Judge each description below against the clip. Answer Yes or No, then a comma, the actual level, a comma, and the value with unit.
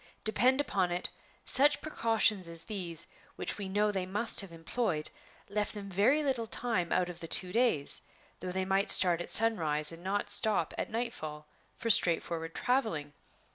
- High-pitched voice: Yes, high, 195 Hz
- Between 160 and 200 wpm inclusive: Yes, average, 175 wpm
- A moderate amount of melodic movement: Yes, average, 5.0 semitones